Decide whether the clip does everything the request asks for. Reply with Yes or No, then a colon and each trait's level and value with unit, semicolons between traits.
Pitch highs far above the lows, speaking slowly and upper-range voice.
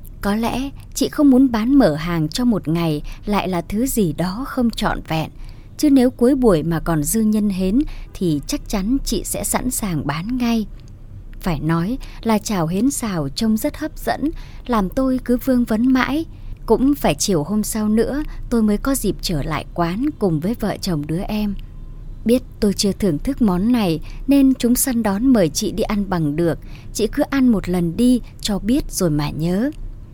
No: wide, 6.9 semitones; average, 200 wpm; high, 210 Hz